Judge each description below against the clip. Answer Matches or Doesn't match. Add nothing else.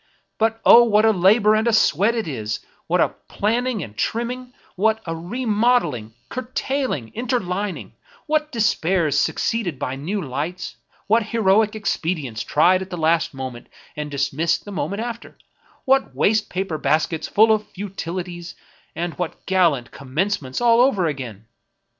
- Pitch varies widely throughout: Matches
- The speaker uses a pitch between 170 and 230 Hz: Matches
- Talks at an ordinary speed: Matches